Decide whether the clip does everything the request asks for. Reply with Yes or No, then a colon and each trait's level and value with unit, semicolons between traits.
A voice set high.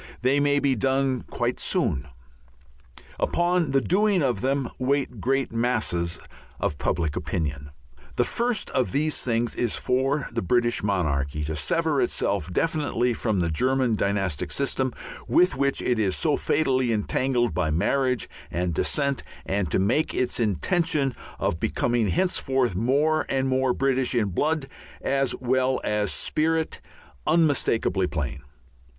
No: low, 125 Hz